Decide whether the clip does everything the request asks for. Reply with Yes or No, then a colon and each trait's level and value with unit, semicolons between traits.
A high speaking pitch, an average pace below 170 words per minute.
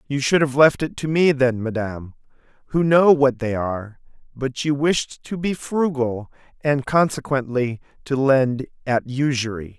No: low, 135 Hz; average, 160 wpm